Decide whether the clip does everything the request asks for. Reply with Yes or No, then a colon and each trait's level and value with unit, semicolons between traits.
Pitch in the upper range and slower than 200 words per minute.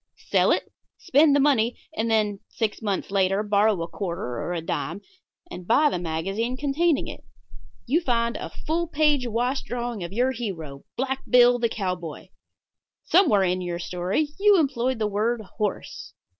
Yes: high, 225 Hz; average, 165 wpm